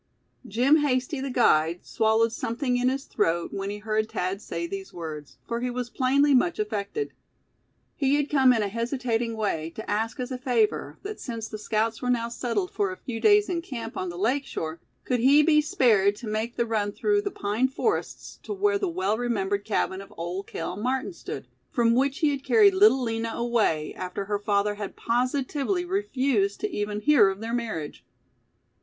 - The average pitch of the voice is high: Yes, high, 230 Hz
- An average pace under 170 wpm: No, average, 195 wpm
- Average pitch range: Yes, average, 4.7 semitones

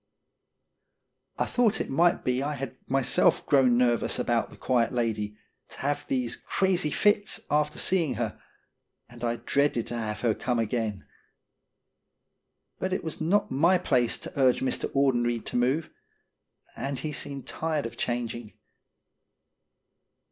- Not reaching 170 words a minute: Yes, average, 140 wpm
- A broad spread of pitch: No, average, 4.0 semitones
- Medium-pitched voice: No, low, 130 Hz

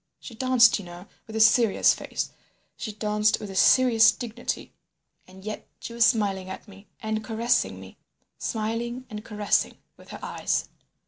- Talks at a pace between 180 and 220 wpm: No, average, 155 wpm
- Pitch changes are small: Yes, narrow, 2.0 semitones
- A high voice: Yes, high, 220 Hz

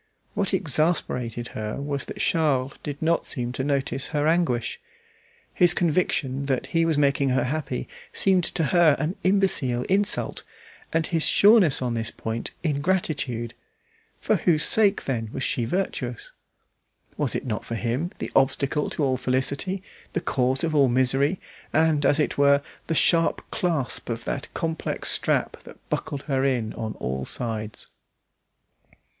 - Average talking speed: Yes, average, 150 wpm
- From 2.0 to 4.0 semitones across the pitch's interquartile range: No, average, 4.6 semitones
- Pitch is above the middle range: No, medium, 140 Hz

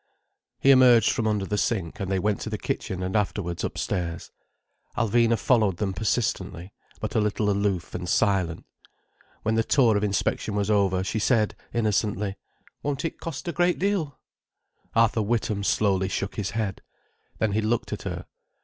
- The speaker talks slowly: No, average, 170 wpm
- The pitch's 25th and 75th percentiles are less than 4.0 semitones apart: Yes, average, 3.0 semitones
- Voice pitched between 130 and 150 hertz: No, low, 105 Hz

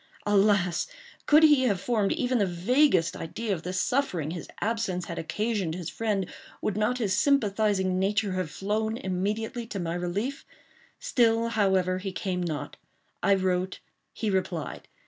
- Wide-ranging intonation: No, average, 3.7 semitones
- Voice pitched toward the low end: No, high, 200 Hz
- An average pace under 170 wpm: Yes, average, 150 wpm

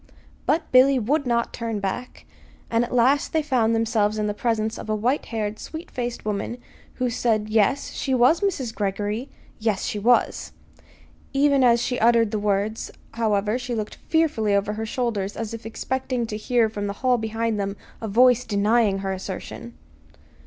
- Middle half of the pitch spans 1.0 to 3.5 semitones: Yes, average, 3.0 semitones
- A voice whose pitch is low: No, high, 225 Hz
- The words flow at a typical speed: Yes, average, 175 wpm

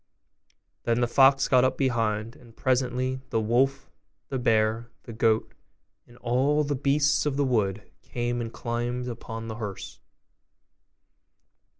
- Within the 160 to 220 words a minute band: No, slow, 135 wpm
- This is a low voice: Yes, low, 120 Hz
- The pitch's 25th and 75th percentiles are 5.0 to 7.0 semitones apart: No, narrow, 2.6 semitones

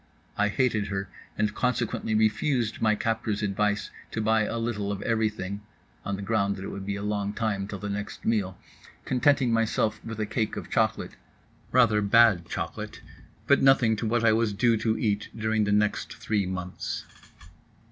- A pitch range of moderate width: No, narrow, 1.9 semitones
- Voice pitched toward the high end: No, low, 105 Hz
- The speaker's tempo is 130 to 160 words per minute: No, average, 175 wpm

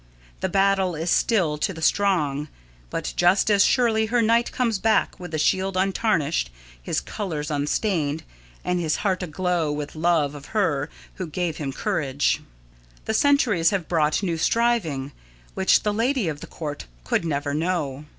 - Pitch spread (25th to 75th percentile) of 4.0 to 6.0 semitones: Yes, average, 5.3 semitones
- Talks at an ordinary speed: Yes, average, 160 wpm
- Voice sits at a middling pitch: Yes, medium, 175 Hz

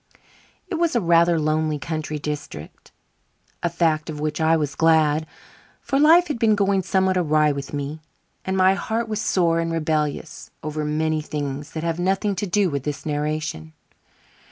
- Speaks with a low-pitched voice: No, medium, 160 Hz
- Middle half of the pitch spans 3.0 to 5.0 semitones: Yes, average, 3.9 semitones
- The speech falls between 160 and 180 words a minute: Yes, average, 170 wpm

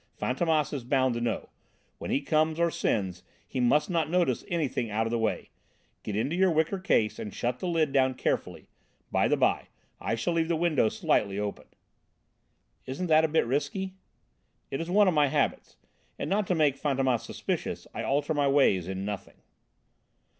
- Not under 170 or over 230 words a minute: Yes, average, 190 wpm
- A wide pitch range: Yes, wide, 5.7 semitones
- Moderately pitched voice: Yes, medium, 145 Hz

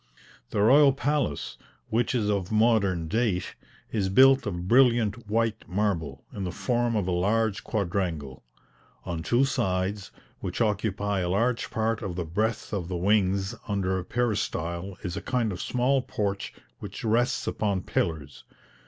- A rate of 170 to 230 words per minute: No, average, 155 wpm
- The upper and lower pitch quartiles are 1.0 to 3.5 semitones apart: No, average, 3.9 semitones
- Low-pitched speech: Yes, low, 105 Hz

